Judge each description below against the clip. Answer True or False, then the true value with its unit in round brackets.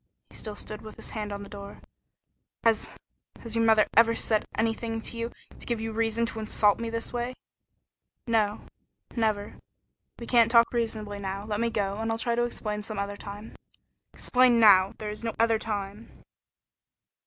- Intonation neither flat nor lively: False (1.8 semitones)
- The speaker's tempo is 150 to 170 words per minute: False (180 wpm)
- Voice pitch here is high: True (220 Hz)